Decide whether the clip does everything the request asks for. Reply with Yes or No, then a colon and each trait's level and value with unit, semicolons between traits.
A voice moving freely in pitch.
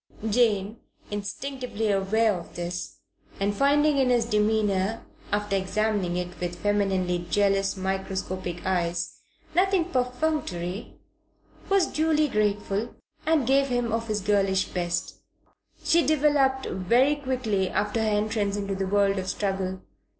No: average, 4.7 semitones